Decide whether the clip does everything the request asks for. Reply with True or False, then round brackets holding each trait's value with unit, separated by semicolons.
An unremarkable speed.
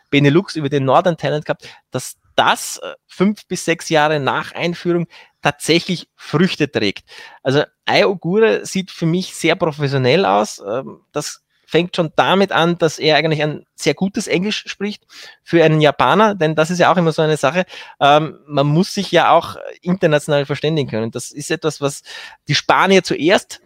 True (165 wpm)